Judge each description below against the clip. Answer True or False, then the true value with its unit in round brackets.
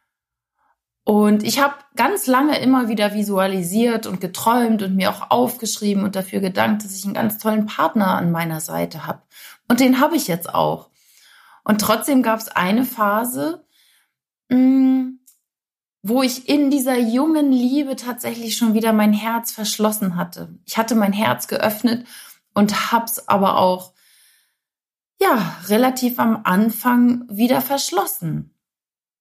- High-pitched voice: True (225 Hz)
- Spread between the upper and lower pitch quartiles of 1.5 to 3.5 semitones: False (3.9 semitones)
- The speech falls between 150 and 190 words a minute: False (140 wpm)